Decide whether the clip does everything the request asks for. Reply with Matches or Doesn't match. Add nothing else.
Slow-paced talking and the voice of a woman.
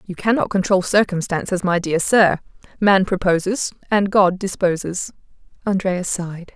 Matches